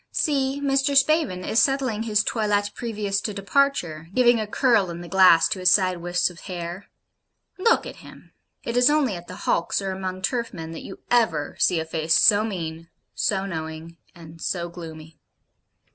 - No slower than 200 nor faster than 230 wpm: No, average, 180 wpm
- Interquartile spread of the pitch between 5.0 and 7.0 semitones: Yes, wide, 5.5 semitones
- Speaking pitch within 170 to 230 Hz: Yes, high, 190 Hz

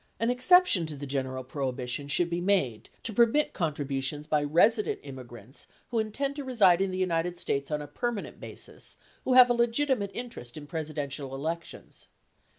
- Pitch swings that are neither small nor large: No, wide, 8.5 semitones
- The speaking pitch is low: No, medium, 165 Hz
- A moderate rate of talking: Yes, average, 165 wpm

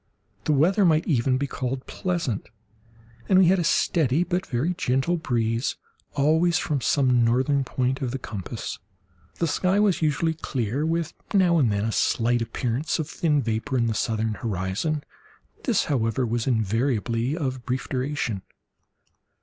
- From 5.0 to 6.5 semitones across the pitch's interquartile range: Yes, wide, 5.4 semitones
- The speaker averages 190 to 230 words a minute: No, average, 150 wpm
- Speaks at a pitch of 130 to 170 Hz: Yes, low, 135 Hz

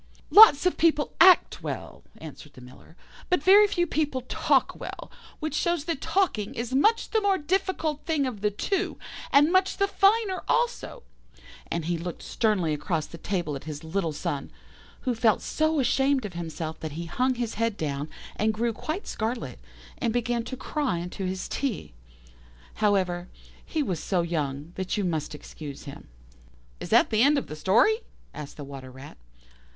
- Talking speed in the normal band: Yes, average, 175 wpm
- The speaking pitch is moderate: No, high, 220 Hz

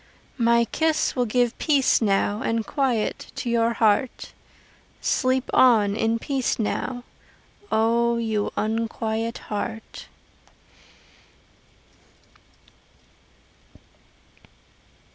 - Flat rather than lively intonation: Yes, narrow, 2.0 semitones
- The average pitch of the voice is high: Yes, high, 230 Hz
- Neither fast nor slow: No, slow, 80 wpm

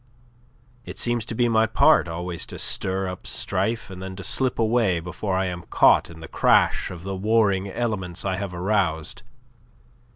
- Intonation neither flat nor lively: Yes, average, 3.6 semitones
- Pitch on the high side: No, very low, 95 Hz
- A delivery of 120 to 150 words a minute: No, average, 175 wpm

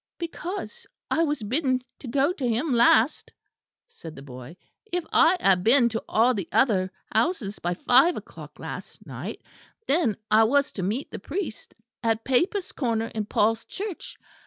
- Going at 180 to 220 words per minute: No, average, 160 wpm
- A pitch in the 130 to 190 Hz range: No, high, 245 Hz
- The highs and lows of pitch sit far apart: Yes, wide, 6.5 semitones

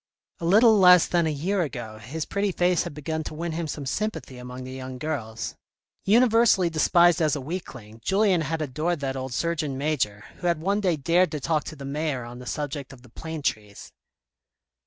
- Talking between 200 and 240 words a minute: Yes, fast, 205 wpm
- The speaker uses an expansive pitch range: No, average, 5.0 semitones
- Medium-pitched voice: Yes, medium, 155 Hz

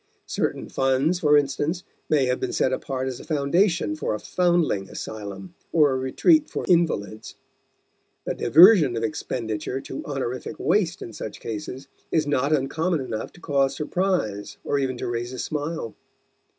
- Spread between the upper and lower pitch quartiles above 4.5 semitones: Yes, average, 5.1 semitones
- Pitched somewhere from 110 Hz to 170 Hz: Yes, medium, 140 Hz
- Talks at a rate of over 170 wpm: No, average, 160 wpm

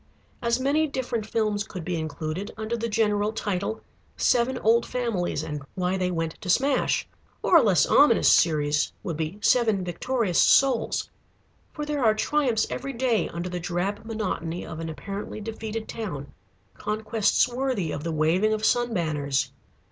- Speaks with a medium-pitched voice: No, high, 210 Hz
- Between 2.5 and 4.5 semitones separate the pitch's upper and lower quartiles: No, average, 5.2 semitones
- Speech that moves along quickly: No, average, 160 wpm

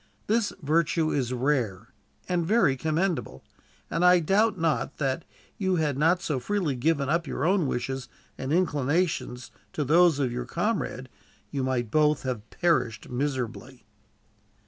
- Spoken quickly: No, average, 145 wpm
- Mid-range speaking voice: Yes, medium, 150 Hz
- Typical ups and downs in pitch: Yes, average, 5.0 semitones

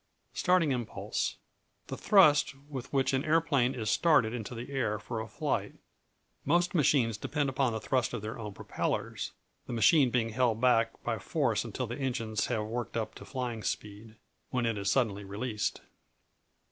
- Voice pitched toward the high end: No, low, 120 Hz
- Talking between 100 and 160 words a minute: No, average, 170 wpm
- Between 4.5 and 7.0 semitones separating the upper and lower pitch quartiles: No, average, 3.6 semitones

